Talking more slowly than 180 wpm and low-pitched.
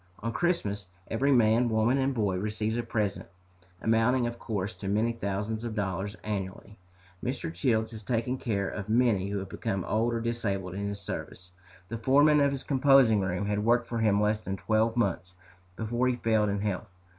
No: average, 190 wpm; low, 110 Hz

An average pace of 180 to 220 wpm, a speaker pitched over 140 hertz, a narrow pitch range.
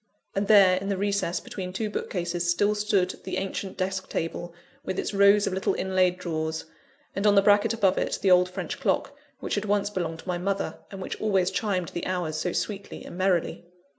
Yes: fast, 205 wpm; high, 190 Hz; narrow, 2.0 semitones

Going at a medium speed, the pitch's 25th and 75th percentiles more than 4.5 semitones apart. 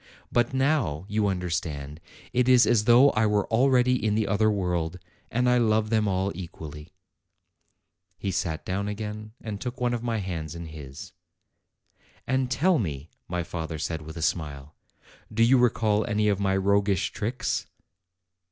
Yes: average, 165 wpm; wide, 5.5 semitones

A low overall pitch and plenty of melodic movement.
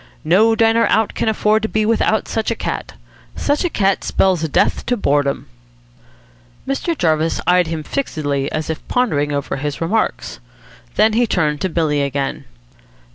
No: medium, 180 Hz; wide, 6.9 semitones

